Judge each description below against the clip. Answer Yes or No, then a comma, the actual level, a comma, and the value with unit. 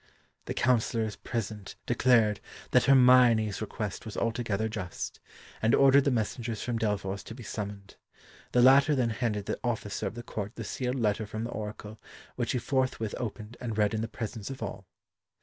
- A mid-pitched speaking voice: No, low, 110 Hz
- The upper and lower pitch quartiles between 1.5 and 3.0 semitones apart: Yes, average, 2.7 semitones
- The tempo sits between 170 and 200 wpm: Yes, average, 180 wpm